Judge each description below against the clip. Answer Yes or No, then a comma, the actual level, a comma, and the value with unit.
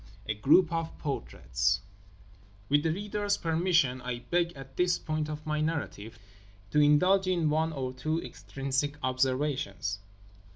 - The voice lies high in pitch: No, medium, 150 Hz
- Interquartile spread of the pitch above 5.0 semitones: No, average, 4.2 semitones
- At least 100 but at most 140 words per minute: Yes, slow, 135 wpm